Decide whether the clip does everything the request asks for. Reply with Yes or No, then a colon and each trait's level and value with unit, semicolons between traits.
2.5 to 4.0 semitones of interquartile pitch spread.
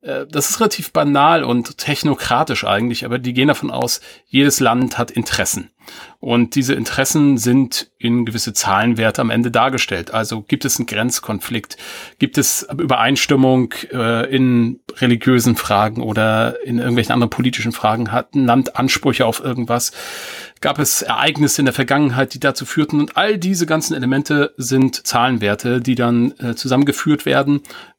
Yes: average, 2.8 semitones